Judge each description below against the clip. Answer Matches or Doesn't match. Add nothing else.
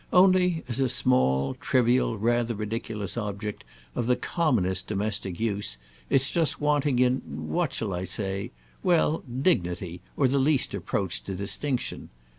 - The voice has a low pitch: Matches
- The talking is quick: Doesn't match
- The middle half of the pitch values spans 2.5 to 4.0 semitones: Doesn't match